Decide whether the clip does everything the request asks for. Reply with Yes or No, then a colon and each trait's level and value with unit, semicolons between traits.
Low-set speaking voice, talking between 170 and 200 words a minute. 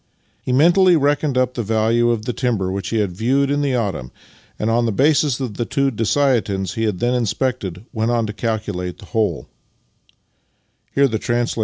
Yes: low, 115 Hz; average, 175 wpm